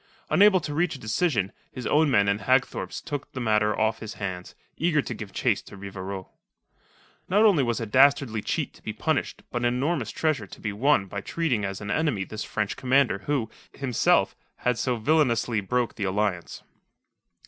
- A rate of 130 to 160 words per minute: No, average, 185 wpm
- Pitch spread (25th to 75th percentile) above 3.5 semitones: Yes, wide, 5.5 semitones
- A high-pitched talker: No, low, 120 Hz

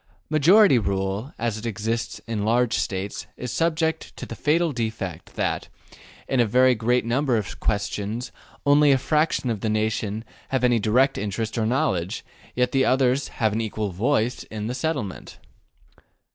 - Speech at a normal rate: Yes, average, 160 wpm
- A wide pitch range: No, average, 3.7 semitones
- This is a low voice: Yes, low, 115 Hz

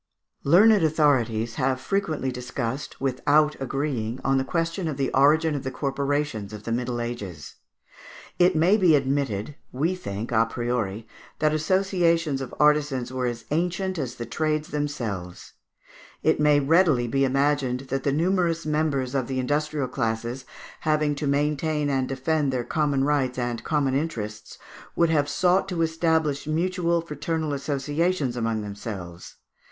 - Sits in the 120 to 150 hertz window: Yes, medium, 140 Hz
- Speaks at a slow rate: No, average, 145 wpm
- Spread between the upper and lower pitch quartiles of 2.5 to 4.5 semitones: Yes, average, 4.0 semitones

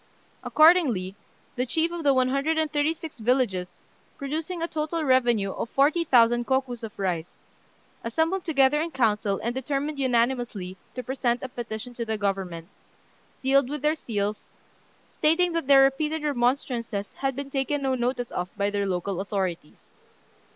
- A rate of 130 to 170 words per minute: Yes, average, 155 wpm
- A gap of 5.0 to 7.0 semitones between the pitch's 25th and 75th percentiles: Yes, average, 5.3 semitones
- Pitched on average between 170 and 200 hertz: No, very high, 255 Hz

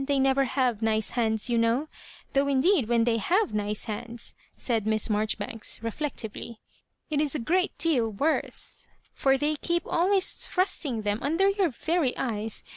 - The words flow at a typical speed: Yes, average, 165 wpm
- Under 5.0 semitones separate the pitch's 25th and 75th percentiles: No, wide, 5.6 semitones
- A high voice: Yes, very high, 255 Hz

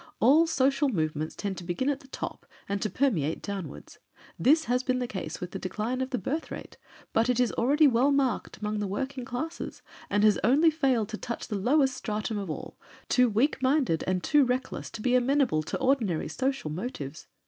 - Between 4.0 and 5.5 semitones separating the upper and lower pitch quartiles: Yes, average, 5.1 semitones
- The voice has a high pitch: Yes, high, 245 Hz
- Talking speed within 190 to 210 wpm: Yes, fast, 205 wpm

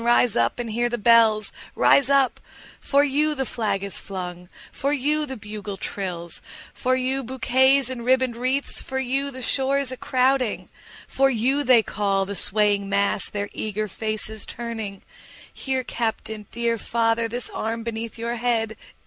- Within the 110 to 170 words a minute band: Yes, average, 150 wpm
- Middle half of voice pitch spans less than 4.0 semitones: Yes, average, 3.6 semitones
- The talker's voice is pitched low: No, high, 235 Hz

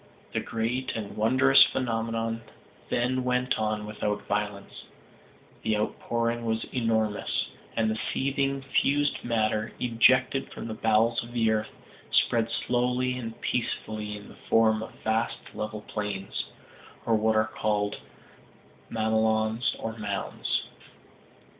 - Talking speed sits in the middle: No, slow, 120 wpm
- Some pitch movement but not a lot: No, narrow, 2.0 semitones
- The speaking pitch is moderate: No, low, 115 Hz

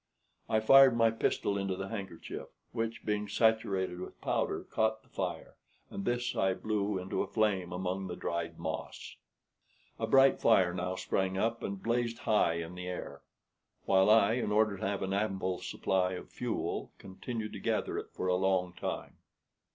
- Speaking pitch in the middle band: No, low, 100 Hz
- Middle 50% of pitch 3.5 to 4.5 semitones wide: No, average, 3.1 semitones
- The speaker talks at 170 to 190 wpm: Yes, average, 175 wpm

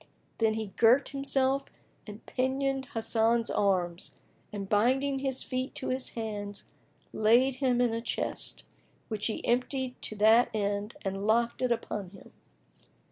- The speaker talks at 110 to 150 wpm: Yes, average, 140 wpm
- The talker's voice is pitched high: Yes, high, 230 Hz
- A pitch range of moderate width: Yes, average, 3.8 semitones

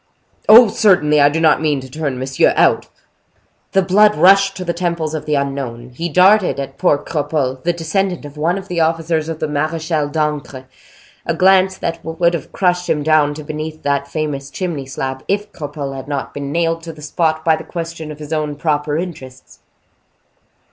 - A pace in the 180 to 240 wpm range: Yes, average, 190 wpm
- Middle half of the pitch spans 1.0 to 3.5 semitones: Yes, average, 3.0 semitones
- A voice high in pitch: No, medium, 155 Hz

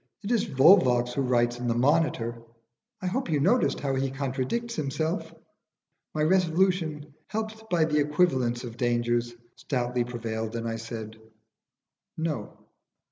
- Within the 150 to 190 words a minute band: No, slow, 135 wpm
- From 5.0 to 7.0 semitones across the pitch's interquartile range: Yes, wide, 5.4 semitones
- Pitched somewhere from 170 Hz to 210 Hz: No, low, 135 Hz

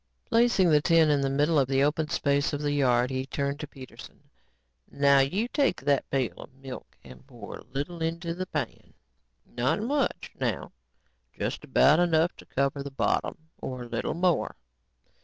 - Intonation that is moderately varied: Yes, average, 3.7 semitones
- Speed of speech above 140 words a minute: Yes, average, 175 wpm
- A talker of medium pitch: Yes, medium, 145 Hz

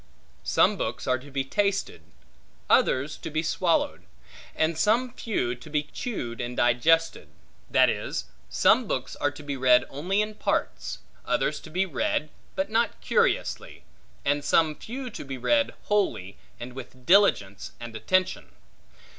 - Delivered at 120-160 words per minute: Yes, average, 150 wpm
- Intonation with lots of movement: Yes, wide, 7.9 semitones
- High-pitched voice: No, medium, 155 Hz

